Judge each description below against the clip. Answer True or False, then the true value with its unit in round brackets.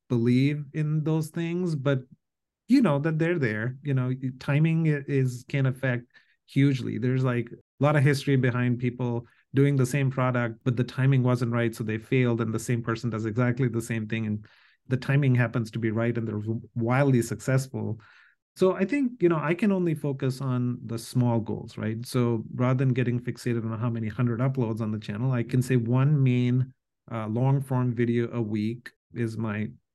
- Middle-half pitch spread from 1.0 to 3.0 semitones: True (2.7 semitones)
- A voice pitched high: False (125 Hz)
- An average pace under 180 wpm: False (195 wpm)